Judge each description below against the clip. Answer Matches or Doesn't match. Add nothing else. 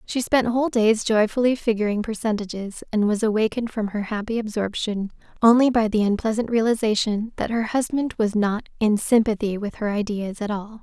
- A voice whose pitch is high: Matches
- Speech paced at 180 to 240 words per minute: Doesn't match